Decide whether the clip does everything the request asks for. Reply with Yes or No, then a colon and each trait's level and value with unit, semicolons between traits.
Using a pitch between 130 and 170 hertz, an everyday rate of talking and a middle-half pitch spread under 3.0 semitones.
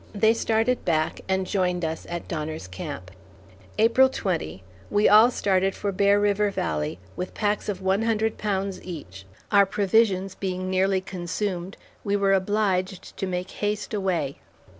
No: high, 190 Hz; average, 150 wpm; narrow, 2.5 semitones